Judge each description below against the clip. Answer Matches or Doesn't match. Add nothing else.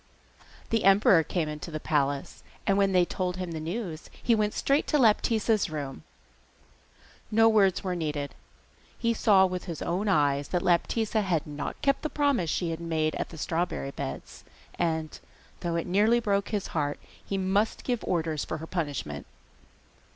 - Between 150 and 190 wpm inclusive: Matches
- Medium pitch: Matches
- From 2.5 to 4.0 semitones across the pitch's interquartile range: Doesn't match